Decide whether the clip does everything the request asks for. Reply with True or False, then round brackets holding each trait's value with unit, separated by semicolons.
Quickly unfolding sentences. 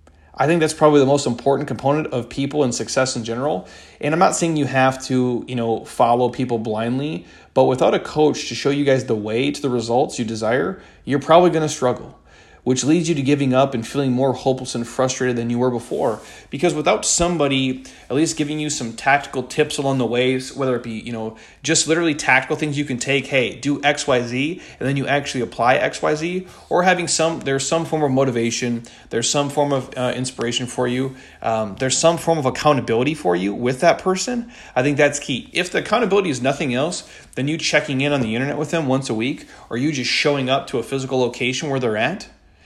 True (220 wpm)